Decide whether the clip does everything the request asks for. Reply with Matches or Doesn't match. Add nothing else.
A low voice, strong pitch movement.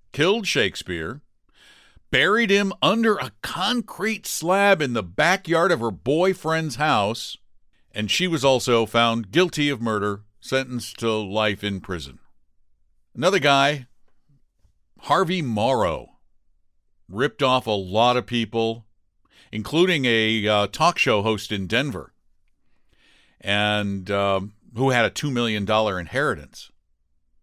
Matches